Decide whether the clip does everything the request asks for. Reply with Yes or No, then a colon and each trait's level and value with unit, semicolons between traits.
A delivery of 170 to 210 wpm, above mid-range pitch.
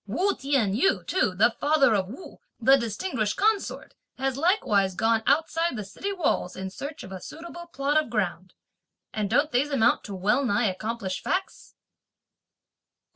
No: average, 160 wpm; very high, 250 Hz